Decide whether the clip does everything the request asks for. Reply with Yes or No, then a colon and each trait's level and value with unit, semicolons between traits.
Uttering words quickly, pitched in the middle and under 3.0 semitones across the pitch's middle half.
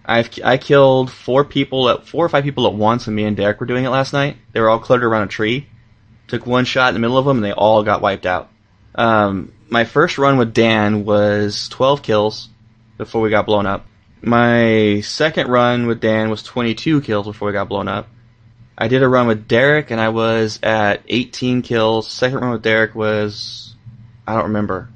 No: fast, 215 wpm; low, 115 Hz; narrow, 2.6 semitones